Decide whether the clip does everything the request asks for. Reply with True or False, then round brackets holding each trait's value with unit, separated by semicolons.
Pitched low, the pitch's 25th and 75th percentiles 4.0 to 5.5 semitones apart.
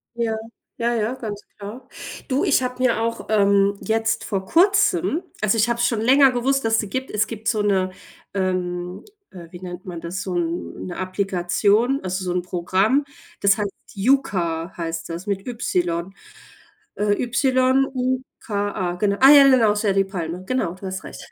False (205 Hz; 4.8 semitones)